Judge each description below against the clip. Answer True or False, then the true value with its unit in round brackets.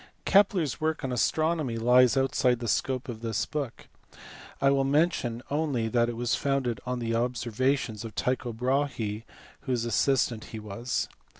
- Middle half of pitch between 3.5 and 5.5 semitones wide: False (3.0 semitones)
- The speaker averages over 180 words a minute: False (170 wpm)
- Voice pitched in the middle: False (125 Hz)